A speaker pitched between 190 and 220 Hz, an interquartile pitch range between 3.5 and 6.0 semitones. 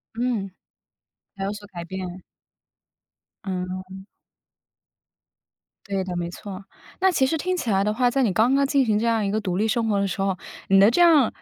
Yes: high, 205 Hz; average, 4.2 semitones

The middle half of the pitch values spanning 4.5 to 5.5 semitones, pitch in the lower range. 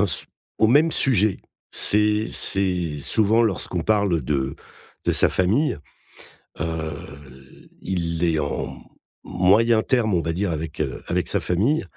Yes: average, 4.9 semitones; very low, 95 Hz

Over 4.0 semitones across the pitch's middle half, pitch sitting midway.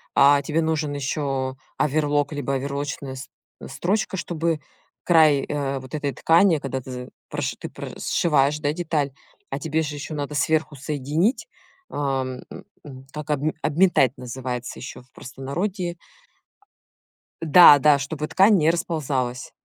No: average, 2.7 semitones; medium, 145 Hz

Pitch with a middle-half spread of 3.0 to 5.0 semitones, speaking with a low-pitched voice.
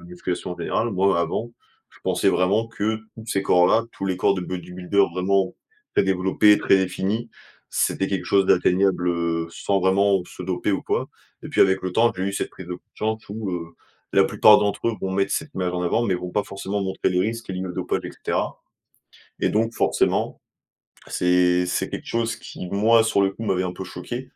No: narrow, 2.4 semitones; very low, 95 Hz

